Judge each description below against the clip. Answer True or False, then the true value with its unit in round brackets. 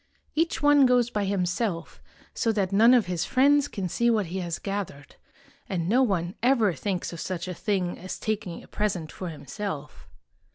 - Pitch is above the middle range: True (195 Hz)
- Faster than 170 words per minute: True (180 wpm)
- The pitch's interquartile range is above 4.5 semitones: True (4.9 semitones)